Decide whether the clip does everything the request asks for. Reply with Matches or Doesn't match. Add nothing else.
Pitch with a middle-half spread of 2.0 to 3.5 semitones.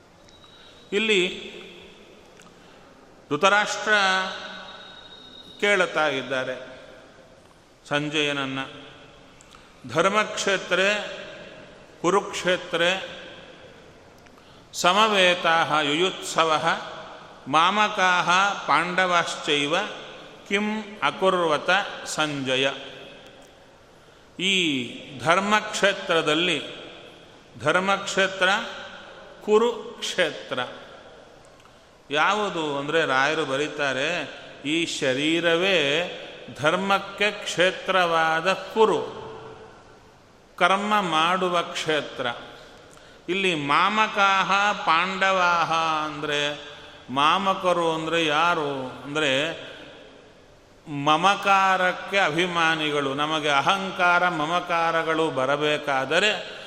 Doesn't match